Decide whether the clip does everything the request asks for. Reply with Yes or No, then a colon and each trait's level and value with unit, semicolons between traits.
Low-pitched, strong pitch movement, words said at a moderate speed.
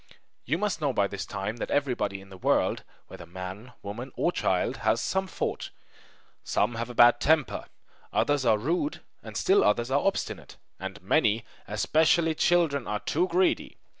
Yes: low, 125 Hz; wide, 7.5 semitones; average, 165 wpm